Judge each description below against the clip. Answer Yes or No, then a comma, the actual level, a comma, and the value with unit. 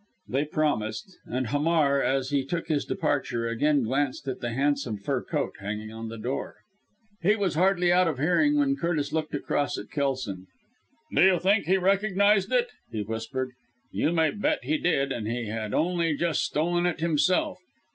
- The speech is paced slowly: No, average, 175 wpm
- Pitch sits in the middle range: Yes, medium, 150 Hz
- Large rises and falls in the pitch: Yes, wide, 5.7 semitones